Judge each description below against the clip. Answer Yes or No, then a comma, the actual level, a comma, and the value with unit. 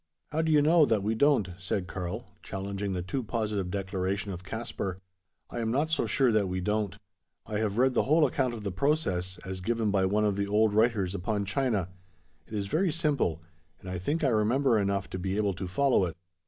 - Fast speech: Yes, fast, 215 wpm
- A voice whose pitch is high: No, low, 105 Hz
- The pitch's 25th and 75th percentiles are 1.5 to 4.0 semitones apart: No, average, 4.5 semitones